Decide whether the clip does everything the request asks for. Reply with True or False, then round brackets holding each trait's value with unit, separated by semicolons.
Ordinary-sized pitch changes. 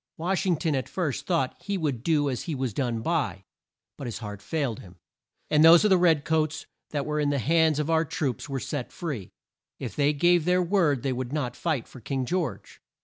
True (4.3 semitones)